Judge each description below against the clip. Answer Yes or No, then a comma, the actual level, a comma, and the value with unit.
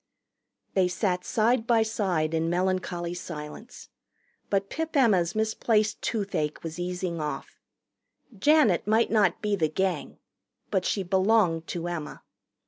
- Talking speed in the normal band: No, slow, 130 wpm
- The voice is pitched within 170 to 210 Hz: Yes, high, 190 Hz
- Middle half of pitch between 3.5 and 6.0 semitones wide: Yes, average, 4.1 semitones